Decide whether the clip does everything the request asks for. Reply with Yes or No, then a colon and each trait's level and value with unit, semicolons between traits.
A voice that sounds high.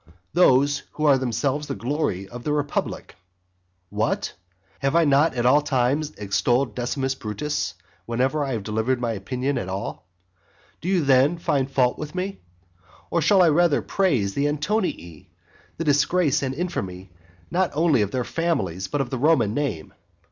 No: low, 135 Hz